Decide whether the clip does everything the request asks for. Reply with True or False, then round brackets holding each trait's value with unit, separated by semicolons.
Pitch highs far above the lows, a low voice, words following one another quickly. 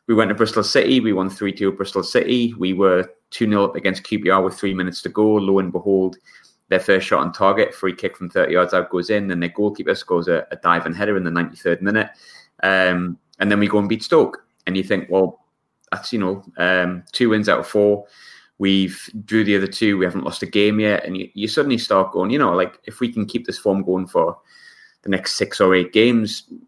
False (2.5 semitones; 100 Hz; 235 wpm)